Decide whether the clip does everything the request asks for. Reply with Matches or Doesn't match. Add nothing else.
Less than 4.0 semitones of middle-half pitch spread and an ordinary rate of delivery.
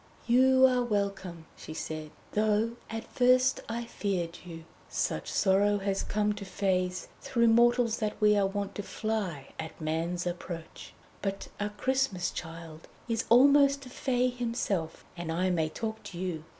Doesn't match